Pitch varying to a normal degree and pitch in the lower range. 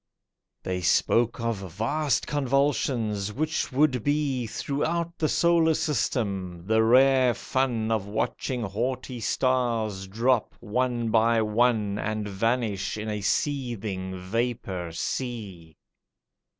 Yes: average, 4.0 semitones; low, 115 Hz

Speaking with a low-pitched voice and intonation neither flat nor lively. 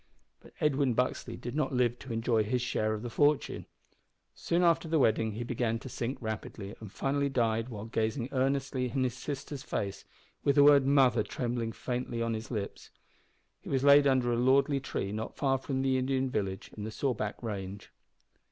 Yes: low, 125 Hz; average, 3.4 semitones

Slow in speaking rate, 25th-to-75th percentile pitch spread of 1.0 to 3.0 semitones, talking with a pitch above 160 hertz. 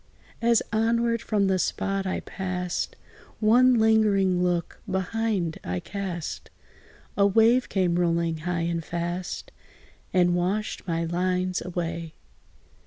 No: slow, 115 wpm; average, 3.7 semitones; medium, 185 Hz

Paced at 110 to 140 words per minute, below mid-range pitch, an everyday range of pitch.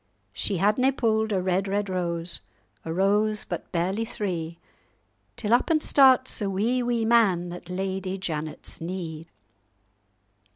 No: slow, 135 wpm; high, 195 Hz; average, 3.8 semitones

